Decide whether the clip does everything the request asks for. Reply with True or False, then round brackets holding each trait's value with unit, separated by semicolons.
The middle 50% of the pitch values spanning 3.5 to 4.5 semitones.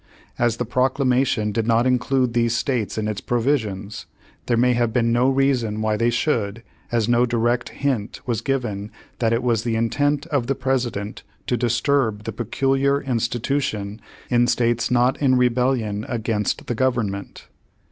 False (2.5 semitones)